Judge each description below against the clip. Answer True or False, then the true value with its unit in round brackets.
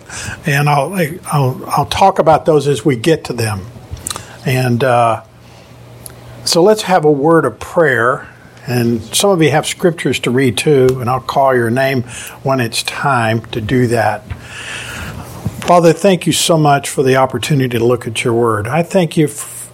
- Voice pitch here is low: True (130 Hz)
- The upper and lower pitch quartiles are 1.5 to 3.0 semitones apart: False (4.4 semitones)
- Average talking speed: True (175 wpm)